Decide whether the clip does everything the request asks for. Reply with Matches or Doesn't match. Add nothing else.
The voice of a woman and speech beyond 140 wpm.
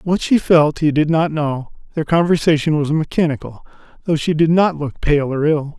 Doesn't match